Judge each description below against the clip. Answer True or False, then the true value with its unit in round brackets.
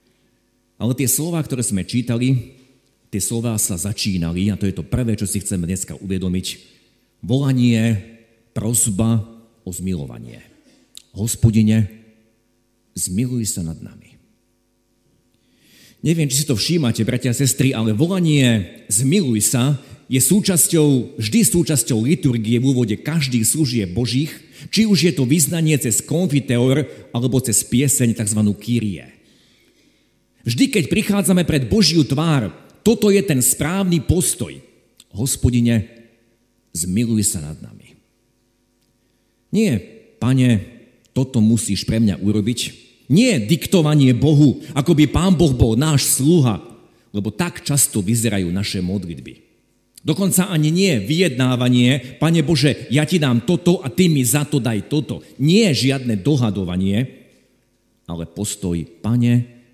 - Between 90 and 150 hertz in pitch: True (120 Hz)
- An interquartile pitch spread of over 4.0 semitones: True (4.8 semitones)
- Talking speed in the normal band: True (125 wpm)